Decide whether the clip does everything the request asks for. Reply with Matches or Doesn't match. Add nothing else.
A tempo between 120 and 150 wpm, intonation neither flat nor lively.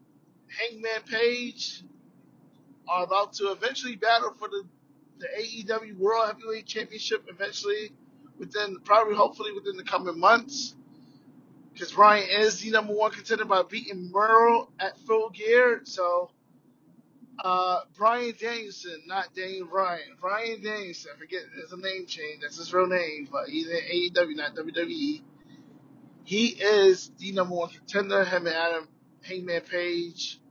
Matches